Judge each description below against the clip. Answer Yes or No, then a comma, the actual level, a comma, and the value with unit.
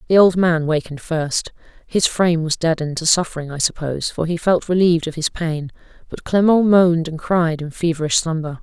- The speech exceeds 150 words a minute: Yes, average, 195 wpm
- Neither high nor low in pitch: Yes, medium, 165 Hz